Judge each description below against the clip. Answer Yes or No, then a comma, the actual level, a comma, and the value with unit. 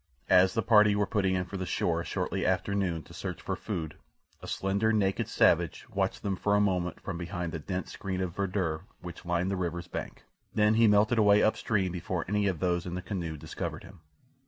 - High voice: No, very low, 95 Hz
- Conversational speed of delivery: No, fast, 215 wpm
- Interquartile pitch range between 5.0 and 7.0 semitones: No, average, 2.7 semitones